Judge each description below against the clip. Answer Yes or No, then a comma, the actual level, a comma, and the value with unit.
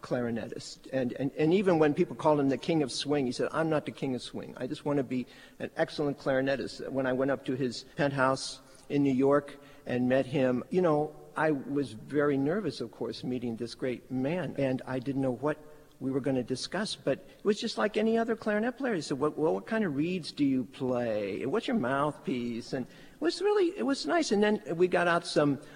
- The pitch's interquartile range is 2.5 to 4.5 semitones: Yes, average, 3.7 semitones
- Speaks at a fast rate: Yes, fast, 235 wpm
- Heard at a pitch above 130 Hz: Yes, medium, 140 Hz